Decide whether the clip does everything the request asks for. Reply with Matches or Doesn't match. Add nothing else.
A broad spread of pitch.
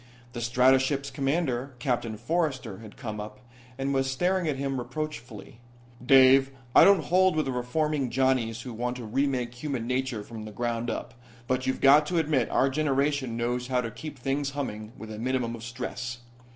Doesn't match